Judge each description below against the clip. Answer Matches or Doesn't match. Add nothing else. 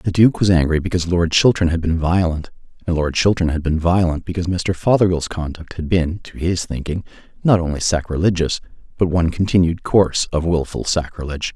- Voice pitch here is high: Doesn't match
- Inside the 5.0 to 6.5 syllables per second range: Matches